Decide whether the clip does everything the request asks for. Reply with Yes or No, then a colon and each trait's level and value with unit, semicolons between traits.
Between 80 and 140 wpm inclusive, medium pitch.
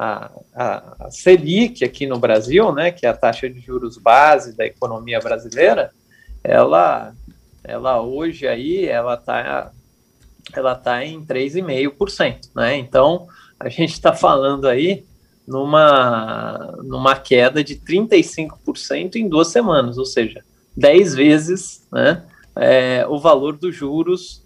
Yes: average, 130 wpm; medium, 150 Hz